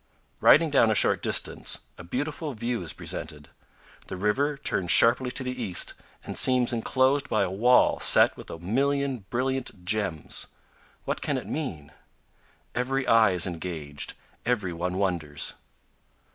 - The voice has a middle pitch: No, low, 115 Hz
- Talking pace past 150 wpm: No, average, 145 wpm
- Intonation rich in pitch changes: Yes, wide, 6.6 semitones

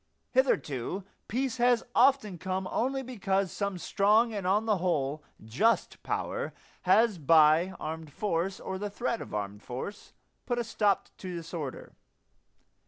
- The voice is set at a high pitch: Yes, high, 195 Hz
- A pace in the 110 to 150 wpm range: Yes, average, 140 wpm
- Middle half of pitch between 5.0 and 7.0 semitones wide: Yes, wide, 5.5 semitones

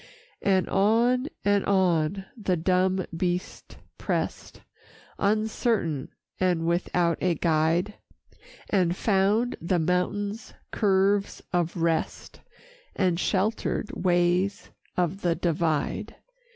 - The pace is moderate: No, slow, 100 wpm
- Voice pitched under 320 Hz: Yes, medium, 185 Hz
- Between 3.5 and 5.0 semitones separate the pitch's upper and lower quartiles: No, average, 2.8 semitones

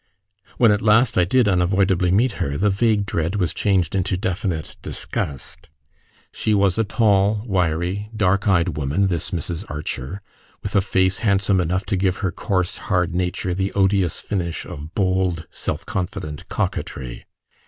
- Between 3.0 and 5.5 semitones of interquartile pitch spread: No, narrow, 2.6 semitones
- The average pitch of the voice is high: No, very low, 95 Hz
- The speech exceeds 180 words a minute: No, average, 155 wpm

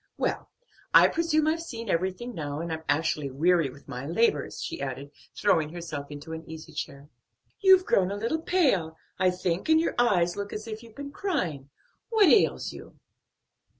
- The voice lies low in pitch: No, medium, 180 Hz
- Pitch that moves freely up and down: Yes, wide, 8.0 semitones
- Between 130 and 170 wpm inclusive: No, average, 180 wpm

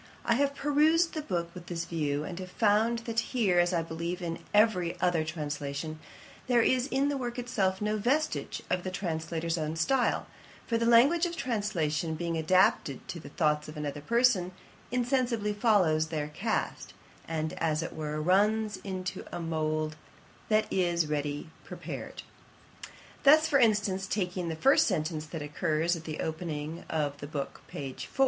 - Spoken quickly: No, average, 170 wpm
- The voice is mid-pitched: Yes, medium, 175 Hz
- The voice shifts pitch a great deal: Yes, wide, 6.4 semitones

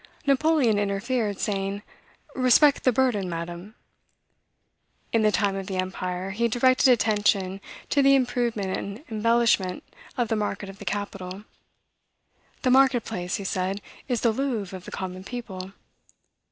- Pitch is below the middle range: No, high, 210 Hz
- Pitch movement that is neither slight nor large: Yes, average, 4.2 semitones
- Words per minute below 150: Yes, average, 140 wpm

